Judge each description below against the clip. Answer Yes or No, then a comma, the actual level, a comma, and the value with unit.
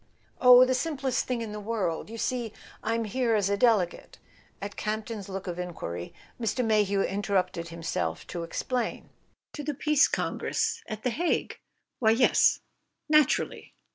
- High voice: Yes, high, 220 Hz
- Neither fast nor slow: Yes, average, 155 wpm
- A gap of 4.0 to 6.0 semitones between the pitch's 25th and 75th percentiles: Yes, average, 4.3 semitones